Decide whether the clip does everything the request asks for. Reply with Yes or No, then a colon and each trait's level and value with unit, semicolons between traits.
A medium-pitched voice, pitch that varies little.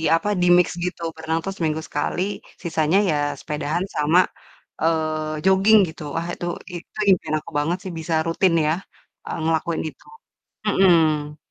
Yes: medium, 160 Hz; narrow, 2.3 semitones